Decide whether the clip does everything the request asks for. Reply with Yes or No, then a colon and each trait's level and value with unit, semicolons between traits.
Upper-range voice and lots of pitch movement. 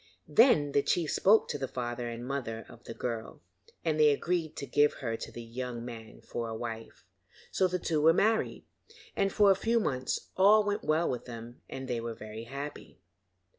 No: low, 135 Hz; wide, 6.2 semitones